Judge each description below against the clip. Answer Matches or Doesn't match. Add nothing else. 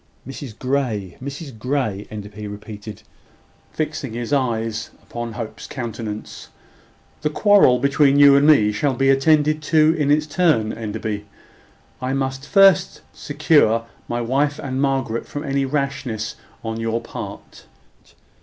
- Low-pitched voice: Matches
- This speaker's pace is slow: Matches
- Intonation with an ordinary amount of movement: Matches